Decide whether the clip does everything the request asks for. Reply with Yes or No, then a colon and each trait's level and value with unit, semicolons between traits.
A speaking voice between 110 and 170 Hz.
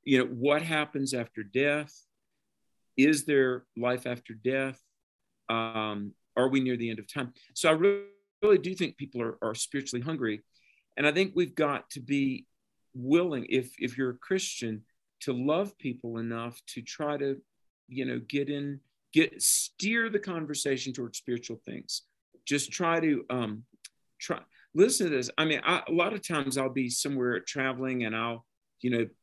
Yes: low, 135 Hz